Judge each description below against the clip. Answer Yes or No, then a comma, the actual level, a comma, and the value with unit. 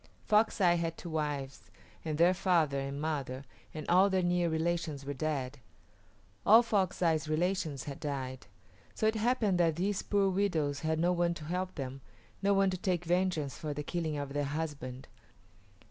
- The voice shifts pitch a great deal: No, average, 4.2 semitones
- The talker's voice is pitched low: No, medium, 165 Hz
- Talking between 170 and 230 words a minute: Yes, average, 175 wpm